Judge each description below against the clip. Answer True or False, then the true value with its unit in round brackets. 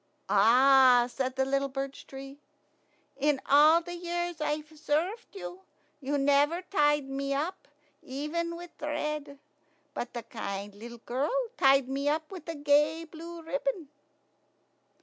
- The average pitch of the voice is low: False (290 Hz)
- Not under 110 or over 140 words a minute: True (135 wpm)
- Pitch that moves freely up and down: False (3.3 semitones)